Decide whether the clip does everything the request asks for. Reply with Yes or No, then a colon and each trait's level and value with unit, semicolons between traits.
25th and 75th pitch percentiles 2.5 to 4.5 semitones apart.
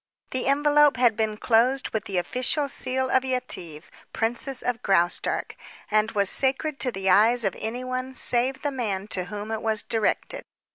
Yes: average, 3.7 semitones